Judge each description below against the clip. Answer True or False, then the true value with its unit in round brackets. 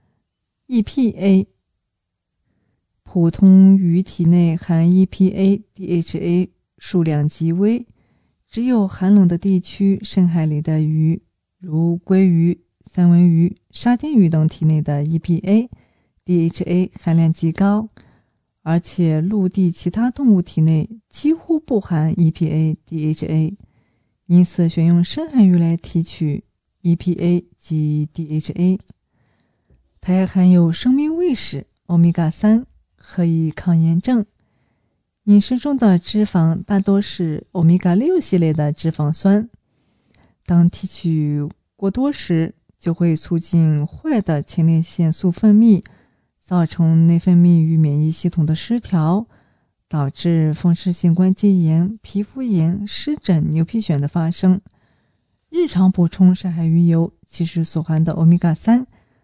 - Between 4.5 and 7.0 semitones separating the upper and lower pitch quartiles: False (3.3 semitones)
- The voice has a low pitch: False (175 Hz)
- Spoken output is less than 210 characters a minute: True (195 characters per minute)